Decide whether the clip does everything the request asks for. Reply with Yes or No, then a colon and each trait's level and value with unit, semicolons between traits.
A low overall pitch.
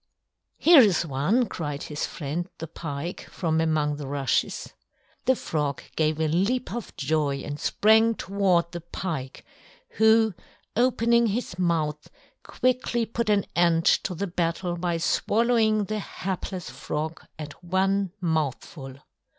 No: medium, 175 Hz